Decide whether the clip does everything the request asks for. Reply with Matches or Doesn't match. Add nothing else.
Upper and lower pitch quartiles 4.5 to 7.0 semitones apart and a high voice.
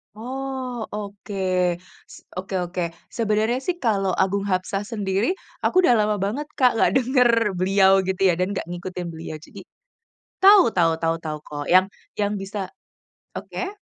Matches